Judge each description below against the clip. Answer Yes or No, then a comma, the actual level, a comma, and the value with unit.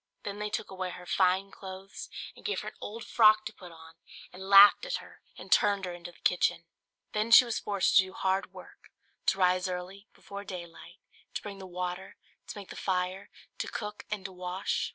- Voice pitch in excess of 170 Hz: Yes, high, 190 Hz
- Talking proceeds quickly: Yes, fast, 210 wpm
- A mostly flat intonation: Yes, narrow, 2.1 semitones